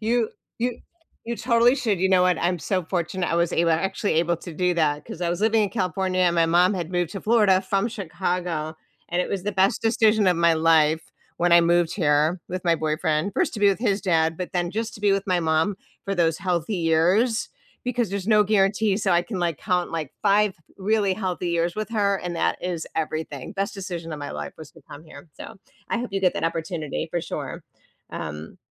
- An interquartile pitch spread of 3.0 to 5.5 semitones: Yes, average, 3.4 semitones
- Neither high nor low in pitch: Yes, medium, 180 Hz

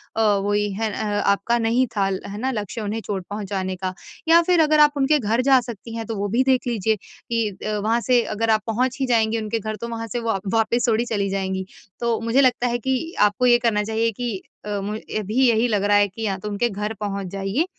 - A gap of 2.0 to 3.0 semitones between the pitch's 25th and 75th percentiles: Yes, average, 2.7 semitones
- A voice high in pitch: Yes, high, 220 Hz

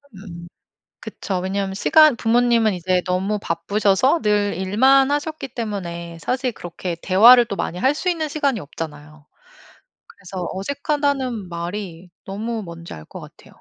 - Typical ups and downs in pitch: No, wide, 6.1 semitones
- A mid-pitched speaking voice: No, high, 200 Hz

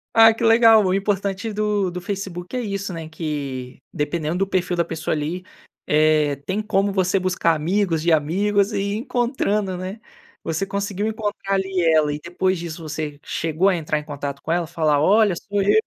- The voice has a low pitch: No, medium, 185 Hz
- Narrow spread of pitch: No, average, 4.2 semitones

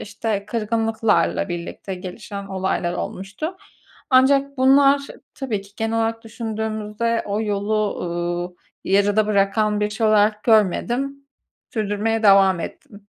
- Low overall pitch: No, high, 215 Hz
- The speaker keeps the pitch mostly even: Yes, narrow, 2.3 semitones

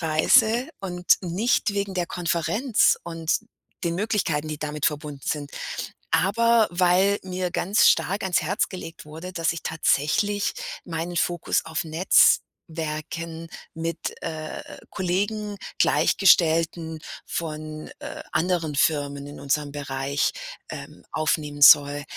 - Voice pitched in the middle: Yes, medium, 165 Hz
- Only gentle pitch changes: No, average, 3.3 semitones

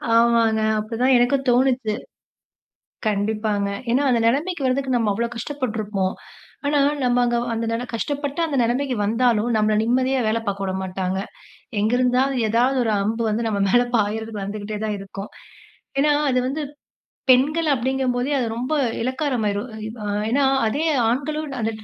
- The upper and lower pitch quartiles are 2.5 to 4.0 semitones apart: Yes, average, 3.5 semitones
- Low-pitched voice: No, high, 235 Hz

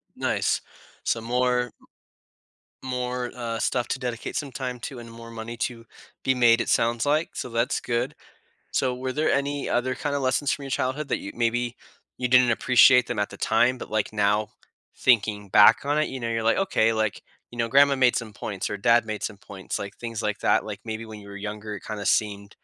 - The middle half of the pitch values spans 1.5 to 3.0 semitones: Yes, narrow, 2.6 semitones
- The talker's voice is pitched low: Yes, low, 120 Hz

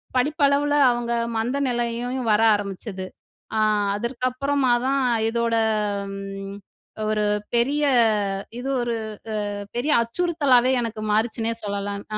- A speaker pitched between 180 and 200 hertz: No, high, 235 Hz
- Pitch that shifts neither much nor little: Yes, average, 3.8 semitones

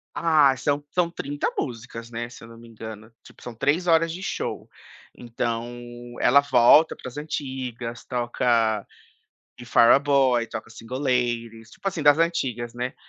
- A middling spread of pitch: Yes, average, 3.6 semitones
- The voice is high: No, low, 125 Hz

